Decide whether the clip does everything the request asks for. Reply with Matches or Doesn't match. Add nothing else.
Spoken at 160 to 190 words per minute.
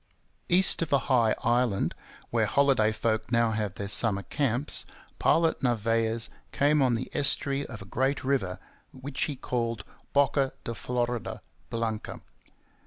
Doesn't match